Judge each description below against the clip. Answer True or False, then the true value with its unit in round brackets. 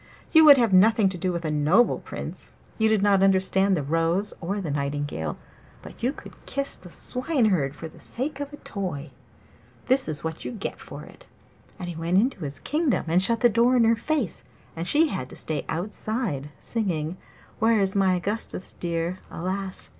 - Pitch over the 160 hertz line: True (190 Hz)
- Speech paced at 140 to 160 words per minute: False (190 wpm)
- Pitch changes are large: True (5.8 semitones)